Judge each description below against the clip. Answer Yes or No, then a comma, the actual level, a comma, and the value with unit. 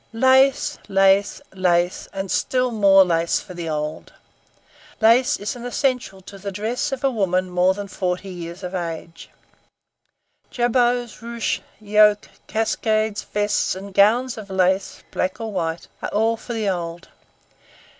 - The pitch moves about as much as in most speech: Yes, average, 3.8 semitones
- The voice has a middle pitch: No, high, 200 Hz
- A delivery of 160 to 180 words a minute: No, average, 145 wpm